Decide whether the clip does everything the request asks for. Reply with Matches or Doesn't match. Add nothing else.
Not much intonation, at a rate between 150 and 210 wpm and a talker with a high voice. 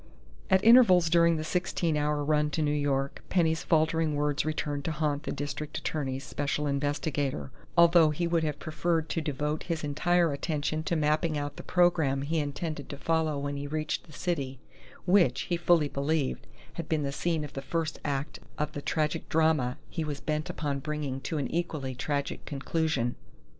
Doesn't match